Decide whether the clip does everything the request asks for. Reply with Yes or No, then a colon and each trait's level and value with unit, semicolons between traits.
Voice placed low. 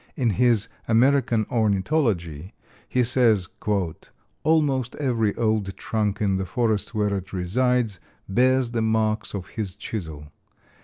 Yes: low, 110 Hz